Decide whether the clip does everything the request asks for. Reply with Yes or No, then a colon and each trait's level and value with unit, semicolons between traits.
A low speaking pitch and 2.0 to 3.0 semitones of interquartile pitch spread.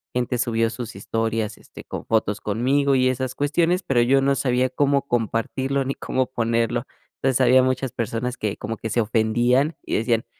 Yes: low, 125 Hz; average, 2.7 semitones